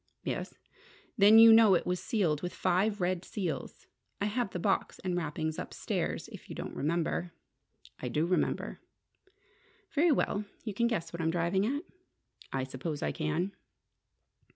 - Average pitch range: Yes, average, 4.2 semitones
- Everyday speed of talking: Yes, average, 155 wpm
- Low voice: No, medium, 180 Hz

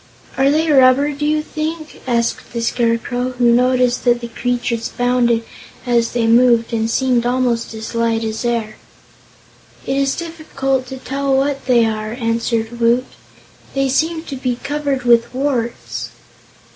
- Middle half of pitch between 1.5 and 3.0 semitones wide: Yes, average, 2.7 semitones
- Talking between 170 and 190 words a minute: No, average, 150 wpm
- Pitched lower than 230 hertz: No, high, 245 Hz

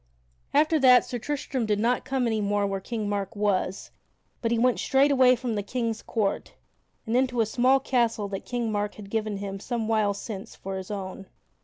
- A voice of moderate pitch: No, high, 225 Hz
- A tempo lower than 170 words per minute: No, average, 200 wpm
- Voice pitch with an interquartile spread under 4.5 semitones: Yes, average, 3.5 semitones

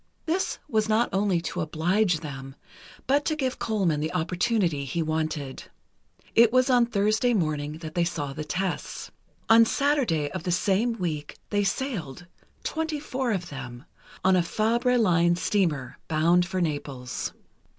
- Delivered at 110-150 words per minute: Yes, average, 145 wpm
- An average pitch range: No, wide, 6.5 semitones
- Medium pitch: Yes, medium, 180 Hz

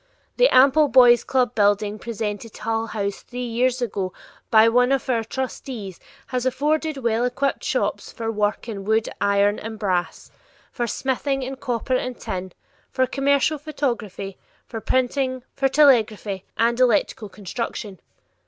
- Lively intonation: No, average, 3.7 semitones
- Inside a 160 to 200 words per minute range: No, average, 145 wpm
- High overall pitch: Yes, high, 235 Hz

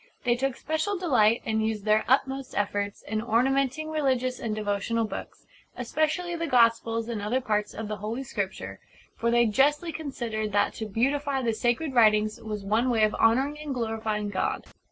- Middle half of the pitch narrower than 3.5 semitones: No, average, 4.0 semitones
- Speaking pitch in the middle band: No, high, 230 Hz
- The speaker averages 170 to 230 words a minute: Yes, average, 175 wpm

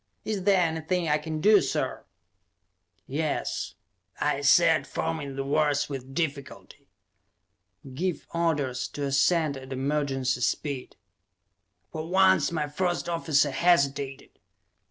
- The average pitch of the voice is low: No, medium, 150 Hz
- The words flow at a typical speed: No, slow, 115 wpm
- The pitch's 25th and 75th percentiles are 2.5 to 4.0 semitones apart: Yes, average, 3.5 semitones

